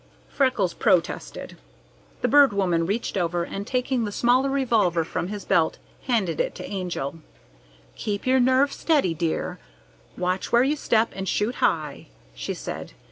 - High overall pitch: Yes, high, 205 Hz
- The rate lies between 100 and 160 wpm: Yes, average, 155 wpm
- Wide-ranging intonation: Yes, wide, 6.5 semitones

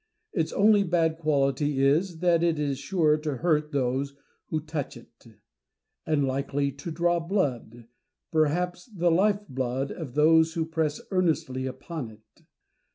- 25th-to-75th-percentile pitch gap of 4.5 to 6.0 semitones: No, average, 3.6 semitones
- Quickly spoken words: No, average, 145 wpm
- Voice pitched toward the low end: No, medium, 155 Hz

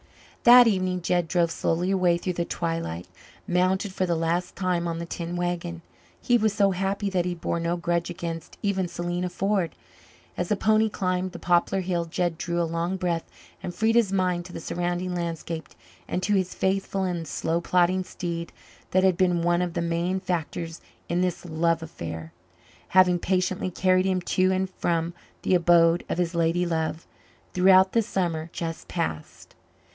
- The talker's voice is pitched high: No, medium, 175 Hz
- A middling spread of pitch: No, narrow, 1.7 semitones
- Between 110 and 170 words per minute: No, average, 180 wpm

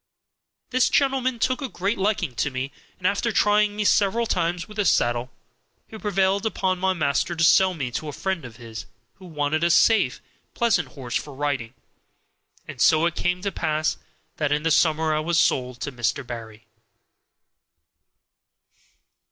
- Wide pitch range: Yes, wide, 6.2 semitones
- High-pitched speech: No, medium, 170 Hz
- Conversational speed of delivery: Yes, average, 170 wpm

